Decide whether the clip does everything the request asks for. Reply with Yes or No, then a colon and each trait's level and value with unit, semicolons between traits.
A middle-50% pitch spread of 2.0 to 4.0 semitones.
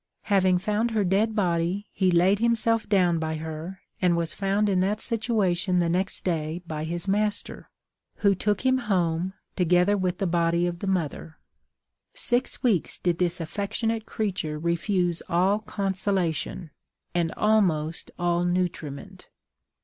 Yes: average, 3.2 semitones